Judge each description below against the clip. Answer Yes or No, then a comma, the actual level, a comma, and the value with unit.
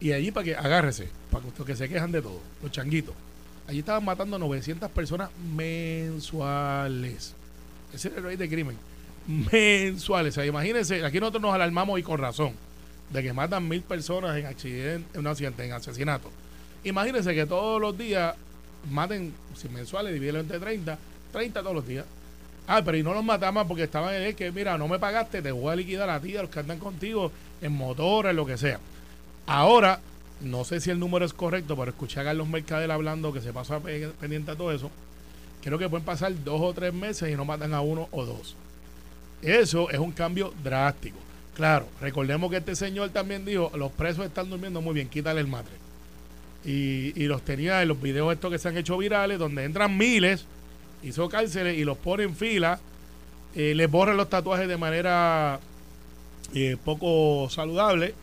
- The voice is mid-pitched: Yes, medium, 155 Hz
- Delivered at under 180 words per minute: No, fast, 190 wpm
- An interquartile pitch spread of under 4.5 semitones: No, wide, 5.4 semitones